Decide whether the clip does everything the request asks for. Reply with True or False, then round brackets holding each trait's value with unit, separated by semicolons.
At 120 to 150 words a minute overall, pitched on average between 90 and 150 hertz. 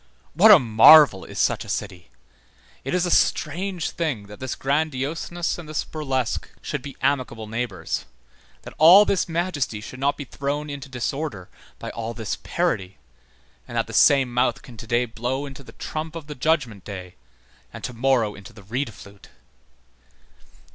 False (170 wpm; 135 Hz)